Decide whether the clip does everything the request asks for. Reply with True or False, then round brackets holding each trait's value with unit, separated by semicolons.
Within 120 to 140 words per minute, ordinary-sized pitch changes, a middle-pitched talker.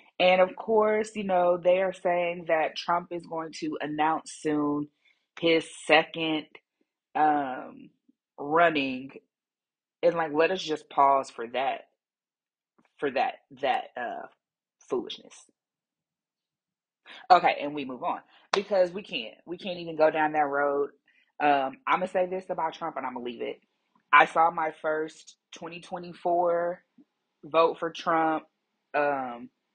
True (135 wpm; 3.0 semitones; 165 Hz)